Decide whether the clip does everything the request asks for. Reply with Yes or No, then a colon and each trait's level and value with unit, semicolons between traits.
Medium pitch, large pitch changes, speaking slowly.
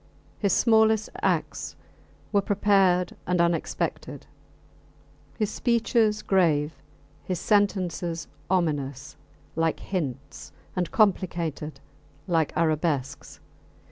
No: medium, 175 Hz; average, 4.4 semitones; slow, 80 wpm